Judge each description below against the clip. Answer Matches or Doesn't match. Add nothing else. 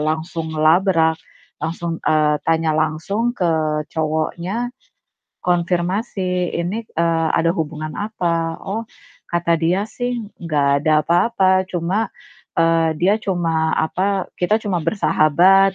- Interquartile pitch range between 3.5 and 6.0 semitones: Doesn't match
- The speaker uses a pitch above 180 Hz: Doesn't match